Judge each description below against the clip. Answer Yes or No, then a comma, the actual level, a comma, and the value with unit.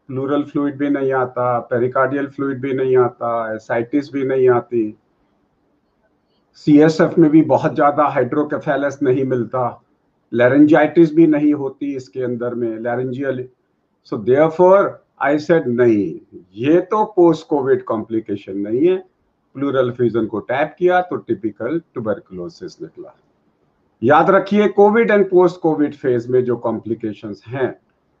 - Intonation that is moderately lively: Yes, average, 4.8 semitones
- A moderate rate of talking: Yes, average, 130 wpm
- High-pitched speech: No, medium, 140 Hz